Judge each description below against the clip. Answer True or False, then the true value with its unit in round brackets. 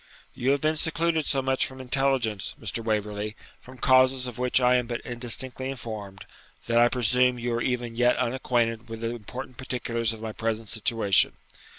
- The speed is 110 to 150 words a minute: False (180 wpm)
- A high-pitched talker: False (120 Hz)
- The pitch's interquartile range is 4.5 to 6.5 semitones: False (2.4 semitones)